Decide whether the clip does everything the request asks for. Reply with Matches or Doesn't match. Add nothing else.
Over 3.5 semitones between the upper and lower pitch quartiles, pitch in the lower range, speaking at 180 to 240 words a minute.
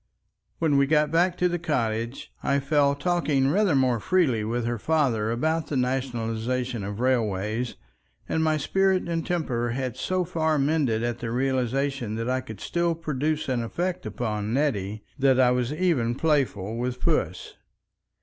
Doesn't match